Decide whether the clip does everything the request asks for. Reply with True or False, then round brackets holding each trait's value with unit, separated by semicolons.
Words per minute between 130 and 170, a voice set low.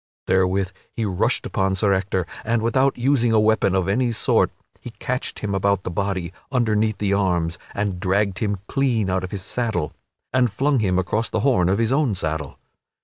False (190 wpm; 100 Hz)